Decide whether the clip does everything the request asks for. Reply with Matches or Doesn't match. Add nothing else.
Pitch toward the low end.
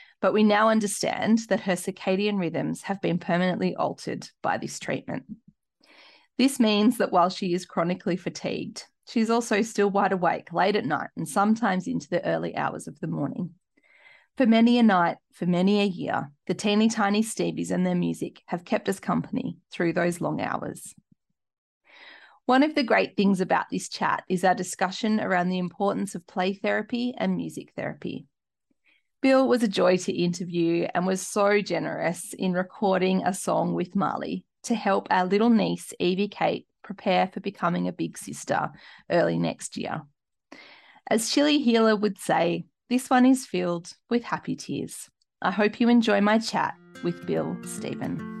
Doesn't match